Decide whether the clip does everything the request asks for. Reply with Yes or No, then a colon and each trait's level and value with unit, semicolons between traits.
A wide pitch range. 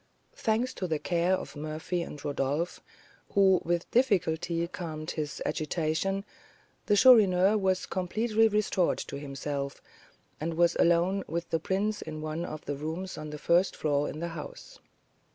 No: average, 3.6 semitones